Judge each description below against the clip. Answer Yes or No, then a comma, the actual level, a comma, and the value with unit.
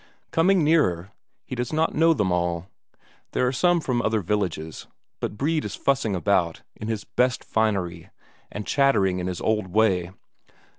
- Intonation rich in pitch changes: Yes, wide, 7.0 semitones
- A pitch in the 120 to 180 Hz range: No, low, 110 Hz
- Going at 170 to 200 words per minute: No, average, 160 wpm